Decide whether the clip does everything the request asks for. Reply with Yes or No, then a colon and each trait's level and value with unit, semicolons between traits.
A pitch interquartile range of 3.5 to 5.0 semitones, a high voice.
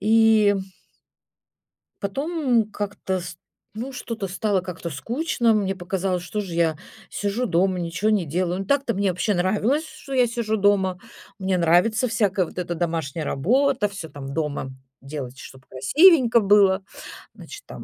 Yes: average, 4.5 semitones; high, 195 Hz